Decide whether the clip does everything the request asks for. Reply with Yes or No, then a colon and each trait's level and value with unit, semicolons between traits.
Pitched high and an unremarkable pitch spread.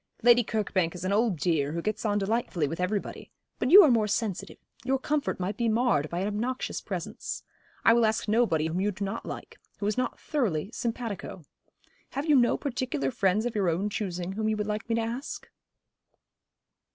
Yes: high, 210 Hz; average, 4.3 semitones